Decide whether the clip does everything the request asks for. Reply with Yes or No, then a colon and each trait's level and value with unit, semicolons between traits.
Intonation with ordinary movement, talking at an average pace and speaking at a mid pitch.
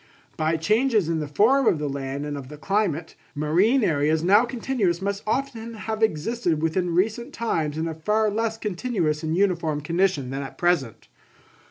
No: wide, 6.1 semitones; average, 170 wpm; medium, 175 Hz